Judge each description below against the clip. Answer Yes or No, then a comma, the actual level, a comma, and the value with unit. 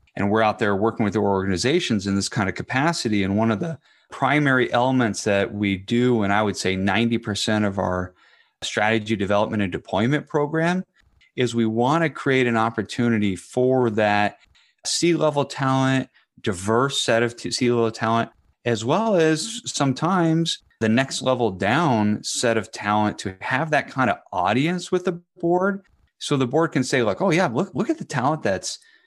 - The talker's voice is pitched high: No, low, 120 Hz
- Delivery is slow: No, average, 175 wpm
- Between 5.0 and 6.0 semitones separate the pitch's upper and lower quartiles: Yes, wide, 5.4 semitones